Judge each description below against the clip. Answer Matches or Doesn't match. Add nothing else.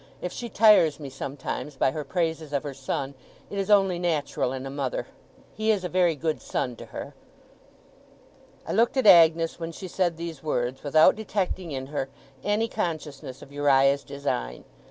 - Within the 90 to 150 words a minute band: Doesn't match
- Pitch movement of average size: Matches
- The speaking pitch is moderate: Matches